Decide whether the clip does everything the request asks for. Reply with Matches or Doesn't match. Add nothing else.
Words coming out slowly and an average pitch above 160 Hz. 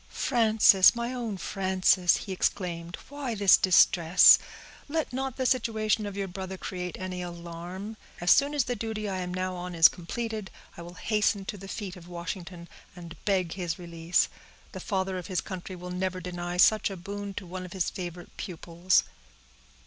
Doesn't match